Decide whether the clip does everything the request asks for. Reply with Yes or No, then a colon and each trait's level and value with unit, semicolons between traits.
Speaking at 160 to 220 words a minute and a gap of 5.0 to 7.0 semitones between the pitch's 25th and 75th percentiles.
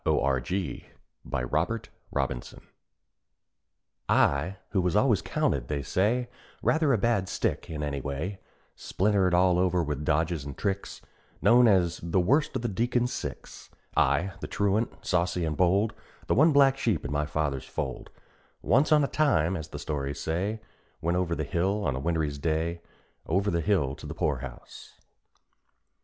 Yes: average, 165 wpm; wide, 5.6 semitones